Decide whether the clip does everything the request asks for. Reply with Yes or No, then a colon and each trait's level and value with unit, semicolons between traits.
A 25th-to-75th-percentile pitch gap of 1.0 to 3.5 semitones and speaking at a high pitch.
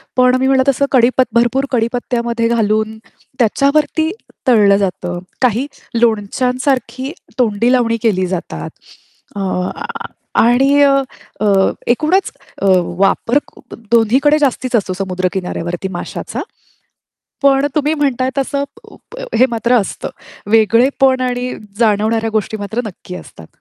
No: average, 4.1 semitones; high, 235 Hz